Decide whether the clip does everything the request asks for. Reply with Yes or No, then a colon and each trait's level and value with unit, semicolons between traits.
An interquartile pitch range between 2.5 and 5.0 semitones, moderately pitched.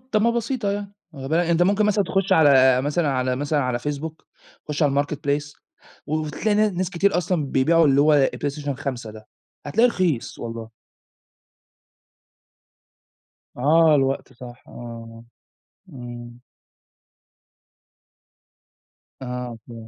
No: wide, 5.4 semitones; medium, 145 Hz